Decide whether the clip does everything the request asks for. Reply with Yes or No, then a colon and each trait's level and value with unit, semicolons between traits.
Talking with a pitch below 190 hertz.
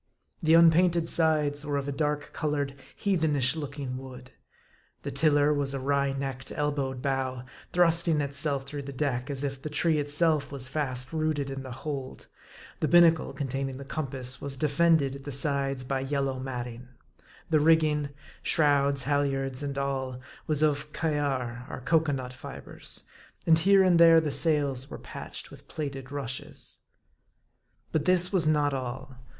Yes: medium, 140 Hz